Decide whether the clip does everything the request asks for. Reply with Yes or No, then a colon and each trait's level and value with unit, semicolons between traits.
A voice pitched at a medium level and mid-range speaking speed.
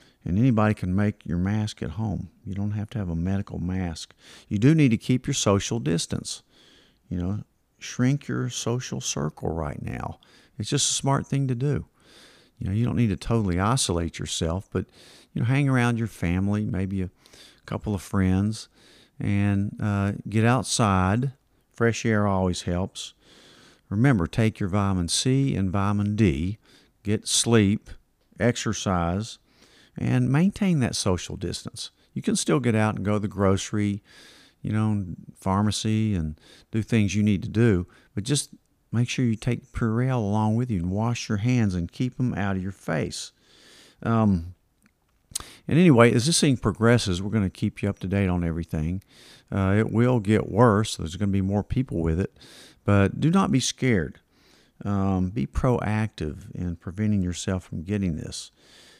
No: low, 105 Hz; average, 170 wpm